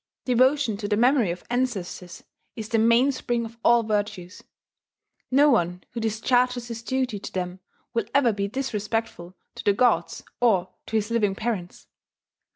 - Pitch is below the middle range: No, high, 225 Hz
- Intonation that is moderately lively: Yes, average, 3.4 semitones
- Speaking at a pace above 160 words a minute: No, average, 155 wpm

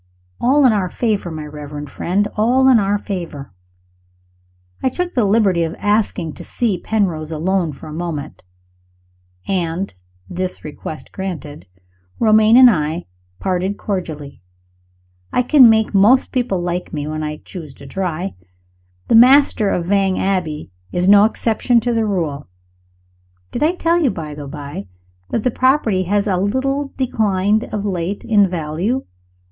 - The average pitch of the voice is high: Yes, high, 195 Hz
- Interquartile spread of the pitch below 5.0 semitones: No, wide, 5.5 semitones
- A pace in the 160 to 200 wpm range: No, average, 150 wpm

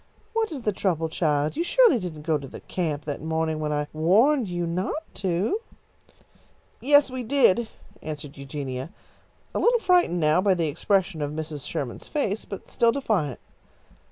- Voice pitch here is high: No, medium, 175 Hz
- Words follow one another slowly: No, average, 165 wpm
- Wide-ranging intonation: Yes, wide, 7.6 semitones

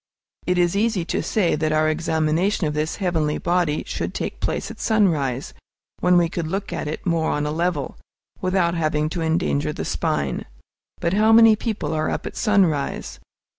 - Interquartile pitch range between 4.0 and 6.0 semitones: No, average, 3.4 semitones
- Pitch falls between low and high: Yes, medium, 170 Hz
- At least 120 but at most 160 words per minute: No, average, 180 wpm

